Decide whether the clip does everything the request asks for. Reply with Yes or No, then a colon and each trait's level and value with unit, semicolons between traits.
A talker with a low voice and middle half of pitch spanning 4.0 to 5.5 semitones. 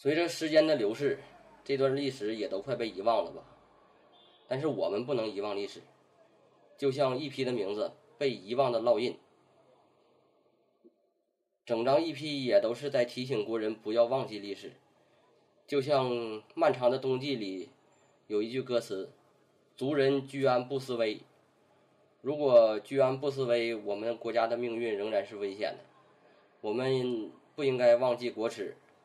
No: low, 130 Hz; average, 3.4 semitones